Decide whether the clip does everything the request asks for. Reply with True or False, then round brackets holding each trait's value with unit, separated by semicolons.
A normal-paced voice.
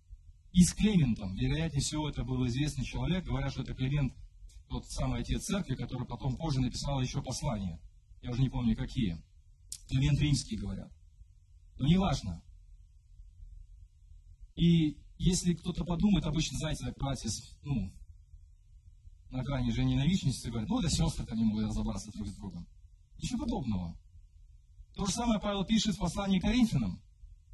True (150 wpm)